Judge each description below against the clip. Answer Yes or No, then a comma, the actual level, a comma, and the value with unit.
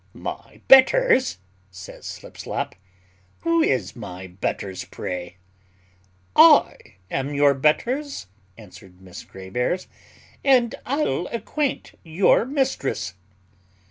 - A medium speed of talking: No, slow, 95 wpm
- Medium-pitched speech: Yes, medium, 145 Hz